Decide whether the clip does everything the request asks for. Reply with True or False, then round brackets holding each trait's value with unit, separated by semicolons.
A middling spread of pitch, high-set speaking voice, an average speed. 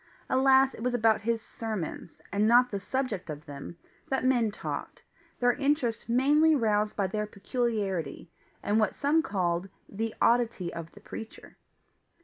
True (4.0 semitones; 225 Hz; 150 wpm)